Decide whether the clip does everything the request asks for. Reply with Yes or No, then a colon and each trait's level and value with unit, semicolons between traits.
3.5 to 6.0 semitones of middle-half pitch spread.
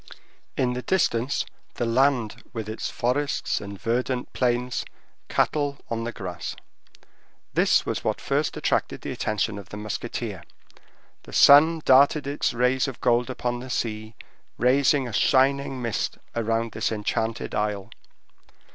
No: average, 3.0 semitones